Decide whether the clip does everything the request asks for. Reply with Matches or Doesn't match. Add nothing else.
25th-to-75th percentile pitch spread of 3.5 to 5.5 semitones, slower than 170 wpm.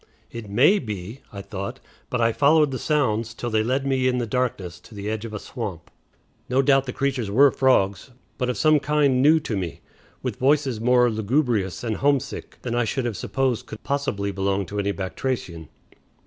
Doesn't match